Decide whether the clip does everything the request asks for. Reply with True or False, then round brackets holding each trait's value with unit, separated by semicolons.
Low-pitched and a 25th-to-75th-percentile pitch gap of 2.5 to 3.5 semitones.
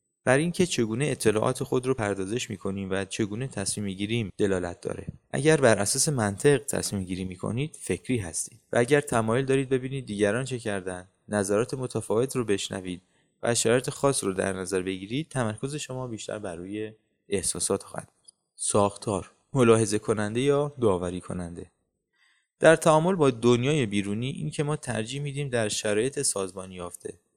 False (110 Hz; 5.4 semitones)